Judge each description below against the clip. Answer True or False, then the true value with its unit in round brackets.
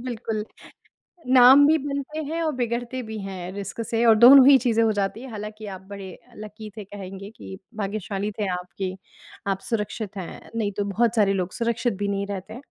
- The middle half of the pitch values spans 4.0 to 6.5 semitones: False (3.5 semitones)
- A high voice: True (215 Hz)